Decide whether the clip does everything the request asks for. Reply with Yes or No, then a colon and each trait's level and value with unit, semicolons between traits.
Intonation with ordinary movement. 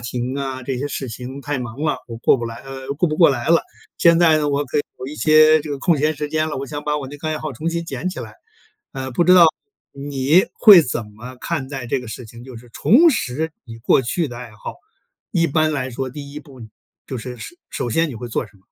Yes: average, 3.9 semitones